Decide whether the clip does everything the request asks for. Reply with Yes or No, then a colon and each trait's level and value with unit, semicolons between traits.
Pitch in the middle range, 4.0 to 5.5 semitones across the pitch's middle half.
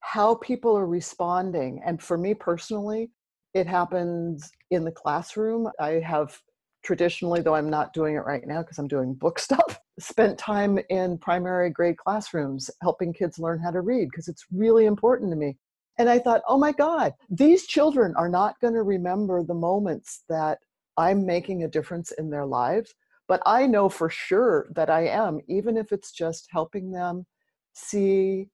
Yes: medium, 180 Hz; average, 4.6 semitones